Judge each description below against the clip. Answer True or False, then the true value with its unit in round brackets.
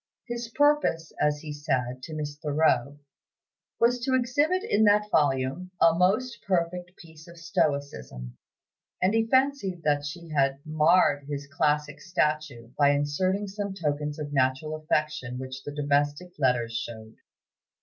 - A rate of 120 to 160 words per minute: True (140 wpm)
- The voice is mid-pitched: True (155 Hz)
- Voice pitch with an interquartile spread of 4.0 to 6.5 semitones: True (4.6 semitones)